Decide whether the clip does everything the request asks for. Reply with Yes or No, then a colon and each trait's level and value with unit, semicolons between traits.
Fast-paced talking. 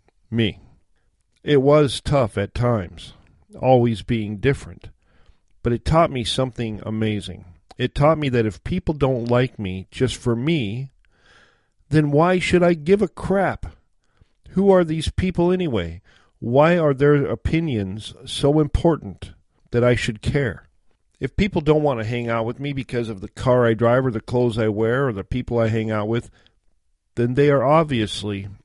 No: average, 170 wpm